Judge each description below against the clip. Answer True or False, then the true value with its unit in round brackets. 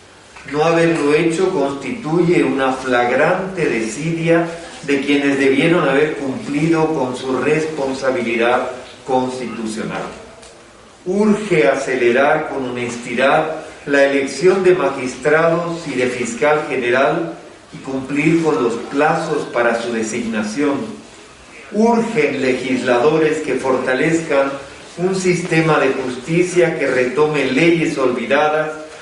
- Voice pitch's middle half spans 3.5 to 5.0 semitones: True (3.9 semitones)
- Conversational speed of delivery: False (100 wpm)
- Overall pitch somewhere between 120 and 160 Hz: True (140 Hz)